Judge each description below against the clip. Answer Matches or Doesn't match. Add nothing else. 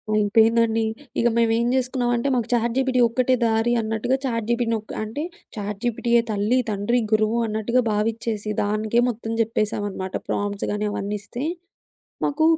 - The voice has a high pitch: Matches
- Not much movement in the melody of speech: Matches